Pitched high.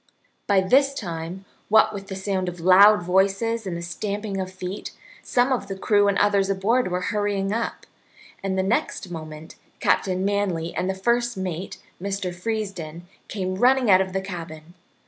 Yes: high, 195 Hz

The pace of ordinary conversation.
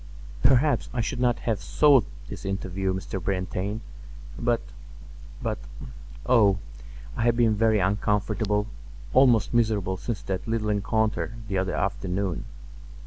No: slow, 120 wpm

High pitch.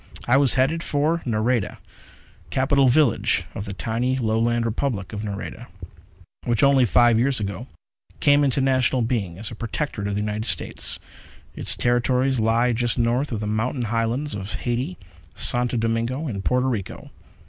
No: low, 120 Hz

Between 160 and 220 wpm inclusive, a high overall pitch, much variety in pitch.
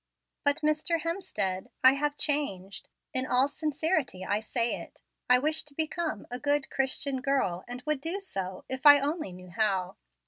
Yes: average, 170 wpm; very high, 275 Hz; wide, 5.8 semitones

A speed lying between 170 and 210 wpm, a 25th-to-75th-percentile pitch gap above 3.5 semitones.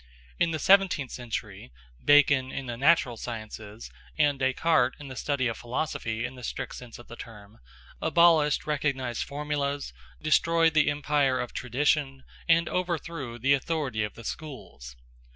No: average, 150 wpm; average, 4.0 semitones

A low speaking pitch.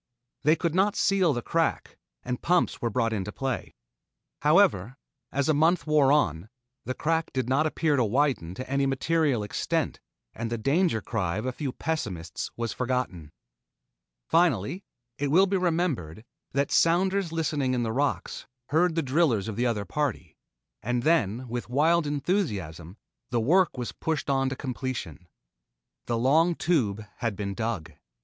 Yes: low, 130 Hz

